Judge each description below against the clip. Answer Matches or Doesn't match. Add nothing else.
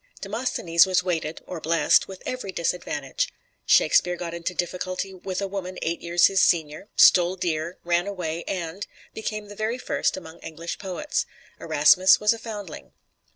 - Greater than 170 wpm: Doesn't match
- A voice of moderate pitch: Matches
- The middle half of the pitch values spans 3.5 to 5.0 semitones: Doesn't match